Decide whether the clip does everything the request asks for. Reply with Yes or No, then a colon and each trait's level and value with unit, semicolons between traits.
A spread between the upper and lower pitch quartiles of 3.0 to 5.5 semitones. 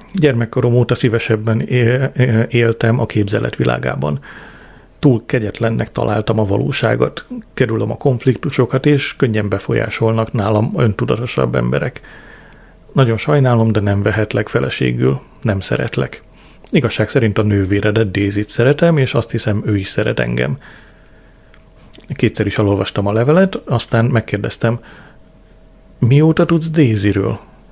Yes: average, 3.9 semitones